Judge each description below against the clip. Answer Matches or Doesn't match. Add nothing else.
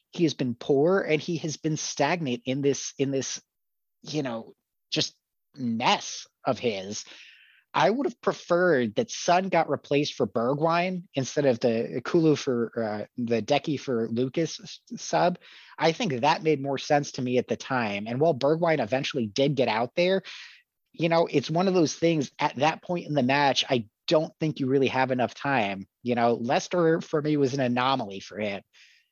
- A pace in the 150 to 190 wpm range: Matches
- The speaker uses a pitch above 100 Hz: Matches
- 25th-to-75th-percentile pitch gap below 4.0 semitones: Doesn't match